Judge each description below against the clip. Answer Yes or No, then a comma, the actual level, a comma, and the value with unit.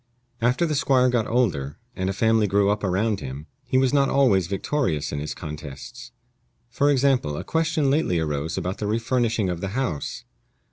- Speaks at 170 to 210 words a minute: Yes, average, 180 wpm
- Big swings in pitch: Yes, wide, 7.1 semitones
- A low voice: Yes, low, 110 Hz